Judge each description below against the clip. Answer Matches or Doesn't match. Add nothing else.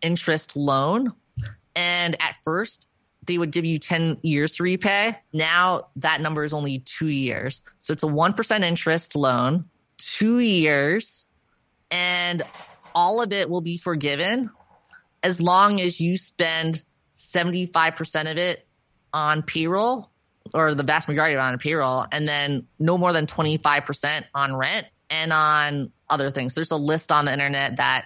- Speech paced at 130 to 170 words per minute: Matches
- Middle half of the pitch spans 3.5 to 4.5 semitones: Doesn't match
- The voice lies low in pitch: Doesn't match